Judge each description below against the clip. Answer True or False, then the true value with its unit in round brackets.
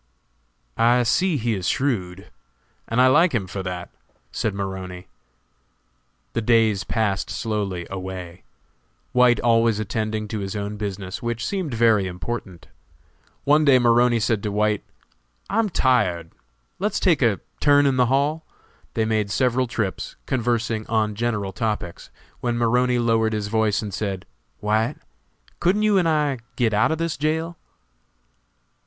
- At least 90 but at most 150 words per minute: True (145 wpm)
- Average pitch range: True (3.9 semitones)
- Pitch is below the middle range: True (115 Hz)